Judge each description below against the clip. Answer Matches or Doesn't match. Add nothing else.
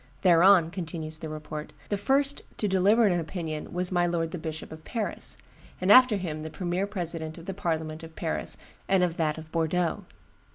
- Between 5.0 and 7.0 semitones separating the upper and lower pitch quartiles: Doesn't match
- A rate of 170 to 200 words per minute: Matches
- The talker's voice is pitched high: Doesn't match